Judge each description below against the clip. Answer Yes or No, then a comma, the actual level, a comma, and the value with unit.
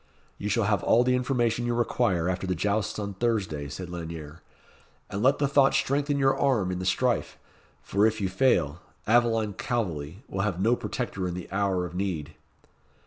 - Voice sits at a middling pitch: No, low, 100 Hz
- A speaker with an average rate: Yes, average, 185 wpm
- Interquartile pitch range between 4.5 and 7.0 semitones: Yes, average, 4.9 semitones